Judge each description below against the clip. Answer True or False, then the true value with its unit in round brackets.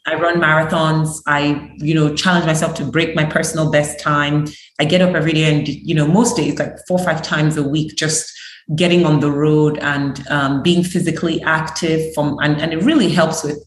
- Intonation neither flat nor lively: False (1.8 semitones)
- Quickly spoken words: True (210 wpm)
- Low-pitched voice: False (155 Hz)